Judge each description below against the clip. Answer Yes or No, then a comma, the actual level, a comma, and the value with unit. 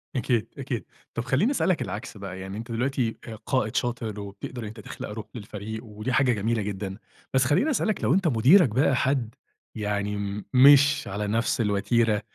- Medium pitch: No, low, 115 Hz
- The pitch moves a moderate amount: Yes, average, 3.9 semitones